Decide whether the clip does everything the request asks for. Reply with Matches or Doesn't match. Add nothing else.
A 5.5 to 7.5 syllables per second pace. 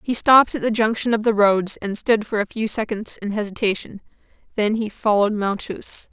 Doesn't match